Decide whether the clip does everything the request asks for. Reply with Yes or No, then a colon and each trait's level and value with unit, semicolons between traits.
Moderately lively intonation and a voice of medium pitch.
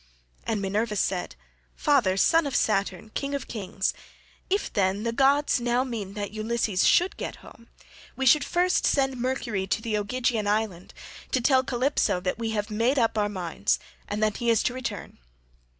No: average, 4.1 semitones; high, 225 Hz